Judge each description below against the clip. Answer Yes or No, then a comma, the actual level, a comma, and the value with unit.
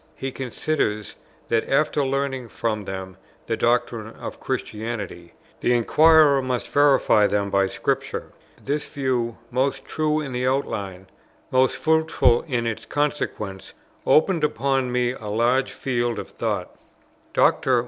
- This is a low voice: Yes, low, 125 Hz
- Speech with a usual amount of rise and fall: Yes, average, 4.0 semitones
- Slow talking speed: Yes, slow, 130 wpm